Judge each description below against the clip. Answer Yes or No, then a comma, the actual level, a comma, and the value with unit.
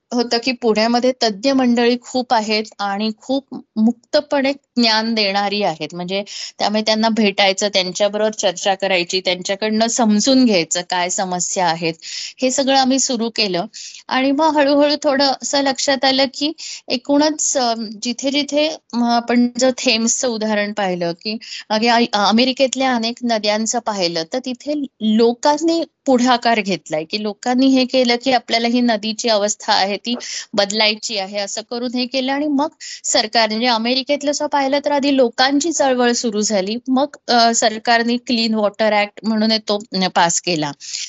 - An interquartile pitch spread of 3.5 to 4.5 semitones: Yes, average, 4.0 semitones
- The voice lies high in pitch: Yes, high, 235 Hz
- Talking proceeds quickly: Yes, fast, 140 wpm